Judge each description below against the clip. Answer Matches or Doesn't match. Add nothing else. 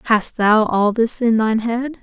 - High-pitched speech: Matches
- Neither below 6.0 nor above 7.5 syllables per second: Doesn't match